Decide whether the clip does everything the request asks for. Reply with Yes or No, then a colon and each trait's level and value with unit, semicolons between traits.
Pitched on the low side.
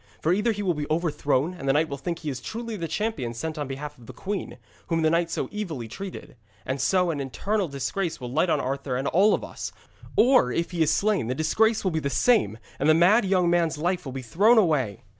No: medium, 160 Hz